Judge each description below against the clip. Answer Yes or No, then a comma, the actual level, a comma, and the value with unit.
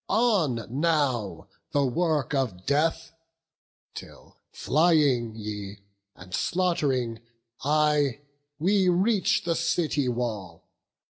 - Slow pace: Yes, slow, 90 wpm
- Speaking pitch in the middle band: Yes, medium, 145 Hz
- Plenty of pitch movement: Yes, wide, 6.2 semitones